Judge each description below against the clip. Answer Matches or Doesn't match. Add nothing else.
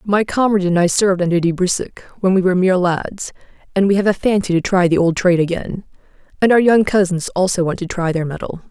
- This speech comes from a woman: Matches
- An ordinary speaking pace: Doesn't match